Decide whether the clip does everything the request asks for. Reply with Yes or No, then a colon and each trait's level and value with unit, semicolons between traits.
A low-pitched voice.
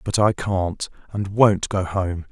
Yes: very low, 95 Hz